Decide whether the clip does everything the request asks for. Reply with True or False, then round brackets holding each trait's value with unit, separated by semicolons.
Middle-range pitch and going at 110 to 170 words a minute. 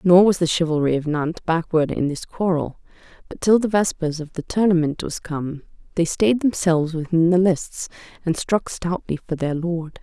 False (170 Hz; 185 wpm)